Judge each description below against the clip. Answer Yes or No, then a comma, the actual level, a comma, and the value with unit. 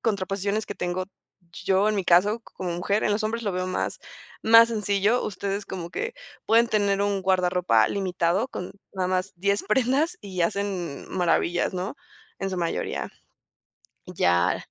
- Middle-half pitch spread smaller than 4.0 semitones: Yes, average, 2.7 semitones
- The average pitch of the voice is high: Yes, high, 195 Hz